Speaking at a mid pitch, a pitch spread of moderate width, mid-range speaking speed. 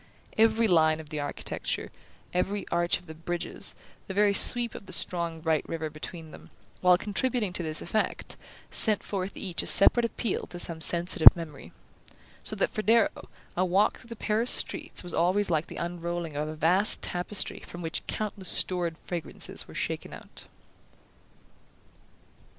Yes: medium, 175 Hz; average, 3.9 semitones; average, 165 wpm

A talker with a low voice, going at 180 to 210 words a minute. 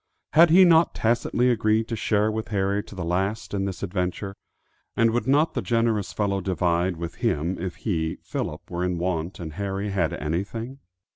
Yes: low, 100 Hz; average, 185 wpm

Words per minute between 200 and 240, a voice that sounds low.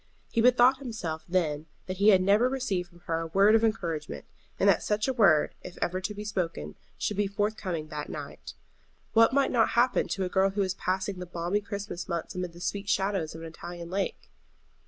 No: fast, 205 wpm; high, 190 Hz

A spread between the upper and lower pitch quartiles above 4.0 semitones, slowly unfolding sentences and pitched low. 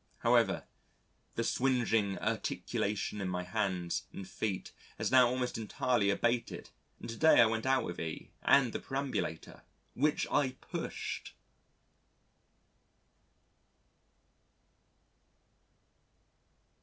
Yes: average, 4.4 semitones; slow, 100 wpm; low, 115 Hz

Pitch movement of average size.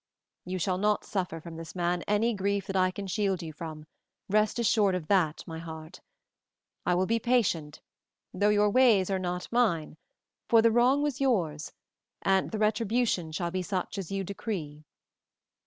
Yes: average, 3.8 semitones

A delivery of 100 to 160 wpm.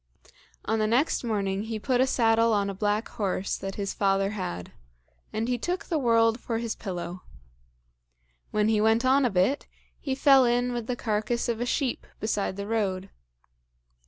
No: average, 180 wpm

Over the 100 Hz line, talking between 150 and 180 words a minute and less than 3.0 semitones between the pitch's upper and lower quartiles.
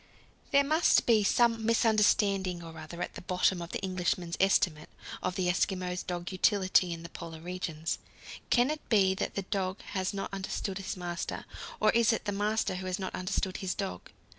No: high, 190 Hz; average, 190 wpm; narrow, 2.6 semitones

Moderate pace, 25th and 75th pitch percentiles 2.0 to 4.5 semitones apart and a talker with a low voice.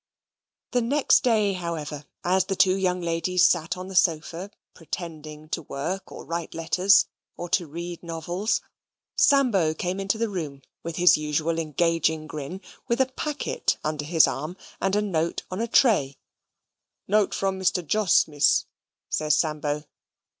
No: average, 155 wpm; average, 3.7 semitones; medium, 175 Hz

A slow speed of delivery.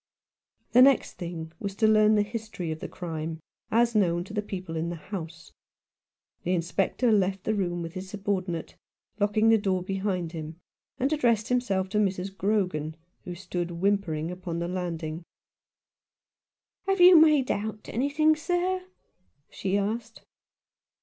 No: average, 150 wpm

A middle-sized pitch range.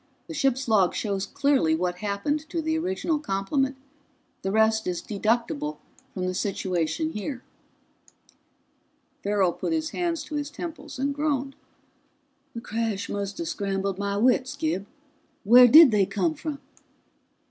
No: wide, 7.0 semitones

